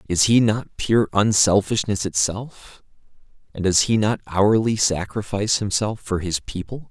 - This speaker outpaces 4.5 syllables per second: No, 4.4 syllables/s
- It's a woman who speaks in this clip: No, male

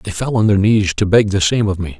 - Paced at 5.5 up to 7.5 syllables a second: Yes, 5.6 syllables/s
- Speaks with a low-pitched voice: Yes, low, 100 Hz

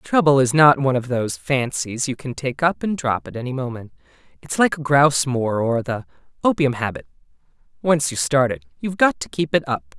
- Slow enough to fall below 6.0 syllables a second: Yes, 5.5 syllables/s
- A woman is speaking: No, male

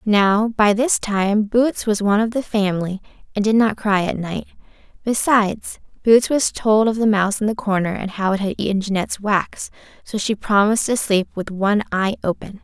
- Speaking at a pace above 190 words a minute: Yes, average, 200 wpm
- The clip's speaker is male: No, female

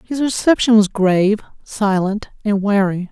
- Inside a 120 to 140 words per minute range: Yes, slow, 135 wpm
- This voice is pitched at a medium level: No, high, 205 Hz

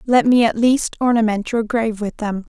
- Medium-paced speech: No, fast, 210 wpm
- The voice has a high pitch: Yes, high, 225 Hz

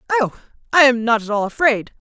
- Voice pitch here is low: No, high, 245 Hz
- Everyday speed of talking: Yes, average, 170 wpm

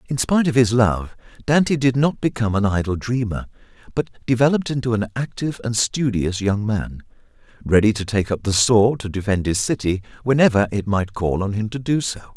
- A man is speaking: Yes, male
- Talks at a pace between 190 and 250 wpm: Yes, average, 195 wpm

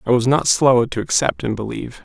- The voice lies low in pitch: Yes, low, 120 Hz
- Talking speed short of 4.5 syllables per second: No, 5.8 syllables/s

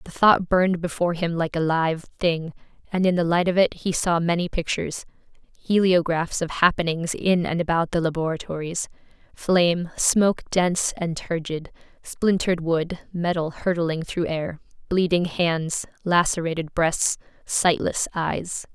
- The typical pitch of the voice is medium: Yes, medium, 170 Hz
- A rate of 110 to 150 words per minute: Yes, average, 140 wpm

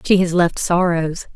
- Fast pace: No, average, 175 wpm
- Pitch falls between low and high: Yes, medium, 175 Hz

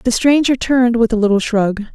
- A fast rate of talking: Yes, fast, 215 wpm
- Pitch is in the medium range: No, high, 230 Hz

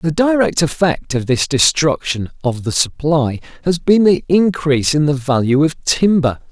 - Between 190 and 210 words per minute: No, average, 165 wpm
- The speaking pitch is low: No, medium, 155 Hz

